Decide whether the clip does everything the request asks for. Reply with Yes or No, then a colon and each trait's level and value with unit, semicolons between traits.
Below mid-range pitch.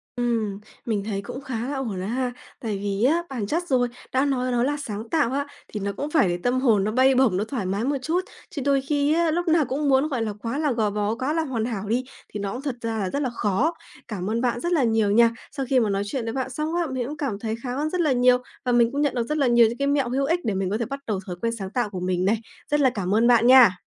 No: high, 245 Hz